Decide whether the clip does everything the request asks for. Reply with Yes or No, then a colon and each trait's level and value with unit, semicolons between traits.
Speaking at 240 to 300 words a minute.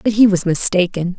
No: average, 200 wpm